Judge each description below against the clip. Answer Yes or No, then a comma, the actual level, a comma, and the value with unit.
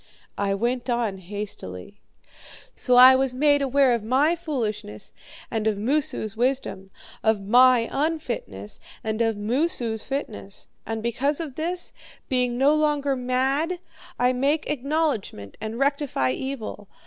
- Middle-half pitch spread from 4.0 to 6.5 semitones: Yes, average, 4.6 semitones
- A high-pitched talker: Yes, very high, 250 Hz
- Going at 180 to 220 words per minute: No, slow, 135 wpm